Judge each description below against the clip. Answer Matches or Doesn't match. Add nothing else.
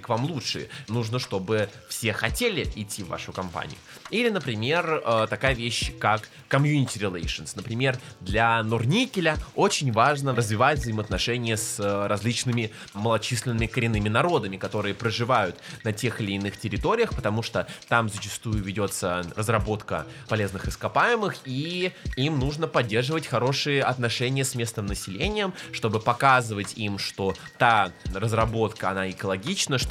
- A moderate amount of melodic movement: Matches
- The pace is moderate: Matches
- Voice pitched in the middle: Doesn't match